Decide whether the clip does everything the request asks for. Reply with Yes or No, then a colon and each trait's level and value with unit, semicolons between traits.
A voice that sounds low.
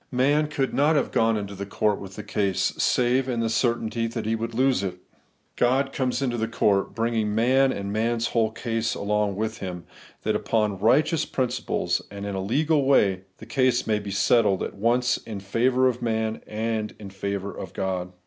Yes: low, 115 Hz